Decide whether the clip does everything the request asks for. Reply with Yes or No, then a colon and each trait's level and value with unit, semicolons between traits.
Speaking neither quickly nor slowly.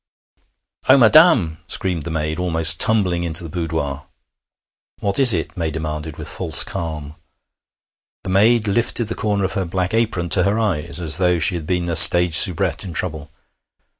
Yes: average, 170 wpm